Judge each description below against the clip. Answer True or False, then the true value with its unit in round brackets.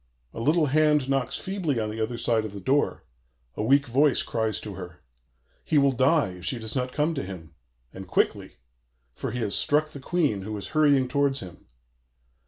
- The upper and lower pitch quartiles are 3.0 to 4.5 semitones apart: False (5.3 semitones)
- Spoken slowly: False (195 wpm)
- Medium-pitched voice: False (130 Hz)